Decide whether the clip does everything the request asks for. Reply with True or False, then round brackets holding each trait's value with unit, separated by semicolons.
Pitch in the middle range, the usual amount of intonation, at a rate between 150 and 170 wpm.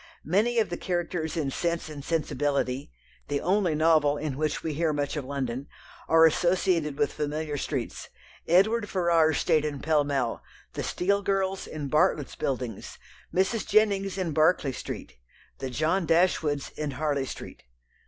True (155 Hz; 3.7 semitones; 155 wpm)